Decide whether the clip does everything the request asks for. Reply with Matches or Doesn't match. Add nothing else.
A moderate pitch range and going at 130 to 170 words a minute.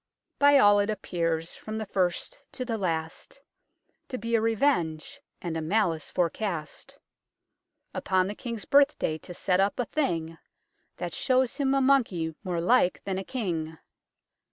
Doesn't match